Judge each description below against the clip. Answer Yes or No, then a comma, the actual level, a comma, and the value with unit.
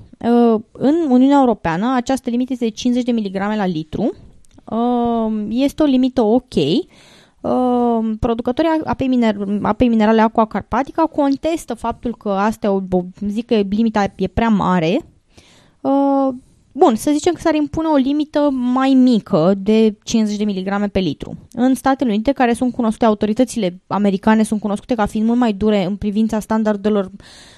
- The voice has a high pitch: Yes, high, 230 Hz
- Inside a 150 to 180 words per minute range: Yes, average, 155 wpm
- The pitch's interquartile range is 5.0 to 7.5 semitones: No, average, 3.6 semitones